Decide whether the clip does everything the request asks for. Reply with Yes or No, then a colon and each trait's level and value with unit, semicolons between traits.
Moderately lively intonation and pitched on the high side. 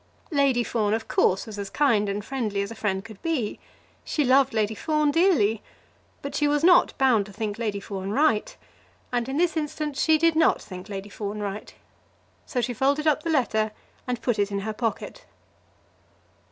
No: wide, 6.0 semitones; high, 235 Hz